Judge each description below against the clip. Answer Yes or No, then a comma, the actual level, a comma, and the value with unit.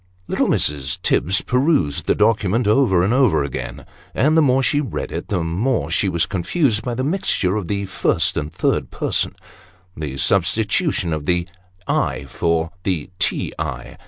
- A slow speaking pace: No, average, 175 wpm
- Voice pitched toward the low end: Yes, very low, 95 Hz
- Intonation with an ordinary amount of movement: No, wide, 7.3 semitones